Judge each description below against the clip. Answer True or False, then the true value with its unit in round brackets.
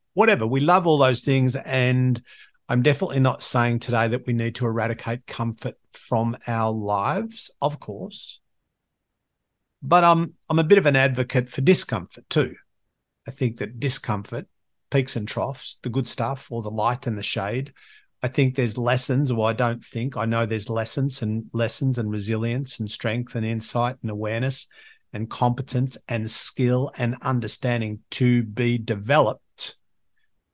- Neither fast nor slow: True (165 wpm)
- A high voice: False (120 Hz)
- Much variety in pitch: False (2.6 semitones)